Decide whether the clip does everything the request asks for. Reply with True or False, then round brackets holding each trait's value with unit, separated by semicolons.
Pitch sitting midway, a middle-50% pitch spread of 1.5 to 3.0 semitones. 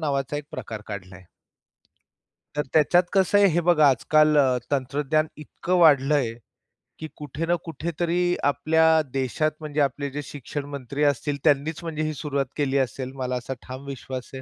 True (145 Hz; 2.7 semitones)